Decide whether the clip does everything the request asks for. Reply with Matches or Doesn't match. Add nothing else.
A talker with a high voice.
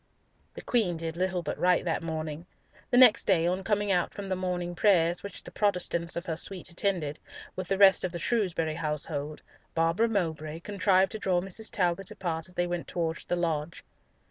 Doesn't match